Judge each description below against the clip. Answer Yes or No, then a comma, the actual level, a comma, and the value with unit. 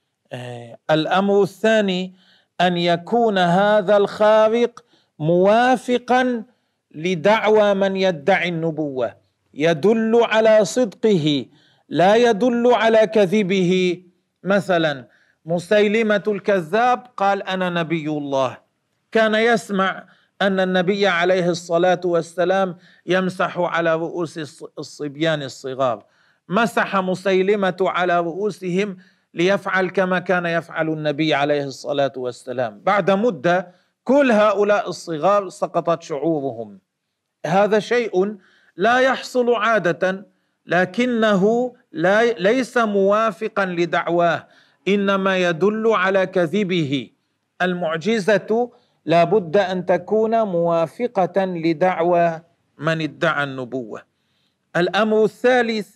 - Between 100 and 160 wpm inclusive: No, average, 90 wpm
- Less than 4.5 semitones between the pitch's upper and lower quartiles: Yes, average, 4.1 semitones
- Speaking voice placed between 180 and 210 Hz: Yes, medium, 185 Hz